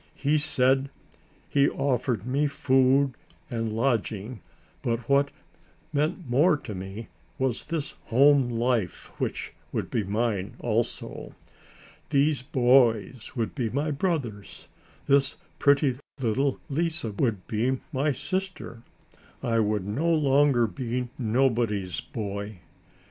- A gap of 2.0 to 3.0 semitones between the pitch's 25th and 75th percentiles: No, average, 3.9 semitones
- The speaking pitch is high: No, low, 125 Hz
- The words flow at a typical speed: No, slow, 115 wpm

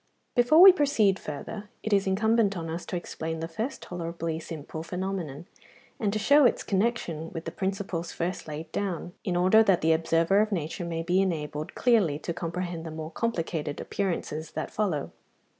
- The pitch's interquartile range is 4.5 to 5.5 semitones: No, average, 3.9 semitones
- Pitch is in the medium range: Yes, medium, 175 Hz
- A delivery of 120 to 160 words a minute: No, average, 175 wpm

